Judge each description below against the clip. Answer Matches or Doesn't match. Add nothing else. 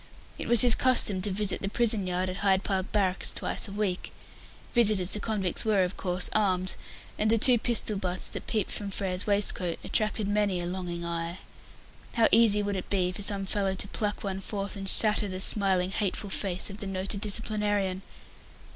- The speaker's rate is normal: Matches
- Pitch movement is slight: Matches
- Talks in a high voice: Matches